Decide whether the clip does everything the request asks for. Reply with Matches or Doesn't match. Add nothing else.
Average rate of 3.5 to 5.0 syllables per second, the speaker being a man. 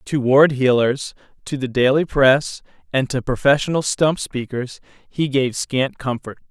Matches